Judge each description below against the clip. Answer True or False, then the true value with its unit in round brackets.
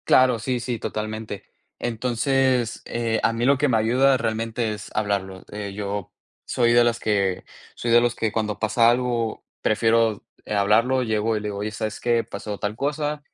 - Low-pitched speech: True (115 Hz)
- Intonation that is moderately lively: False (2.2 semitones)